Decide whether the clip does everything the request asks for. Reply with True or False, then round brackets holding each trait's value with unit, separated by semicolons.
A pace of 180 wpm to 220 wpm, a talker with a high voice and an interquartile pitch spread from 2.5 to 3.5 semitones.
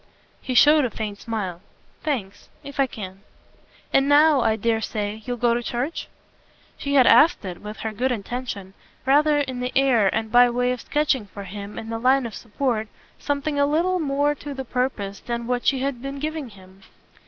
False (195 wpm; 245 Hz; 4.4 semitones)